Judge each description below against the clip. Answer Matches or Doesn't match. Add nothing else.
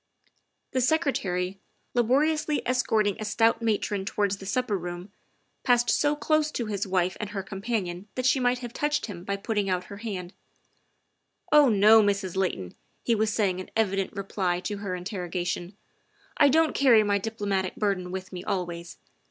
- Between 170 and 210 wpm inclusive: Matches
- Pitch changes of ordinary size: Matches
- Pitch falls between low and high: Doesn't match